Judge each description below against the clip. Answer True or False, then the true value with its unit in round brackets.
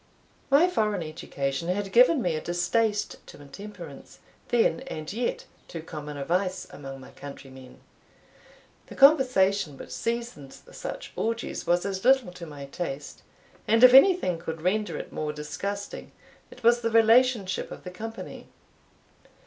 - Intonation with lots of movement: True (6.9 semitones)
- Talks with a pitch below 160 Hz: False (195 Hz)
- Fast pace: False (145 wpm)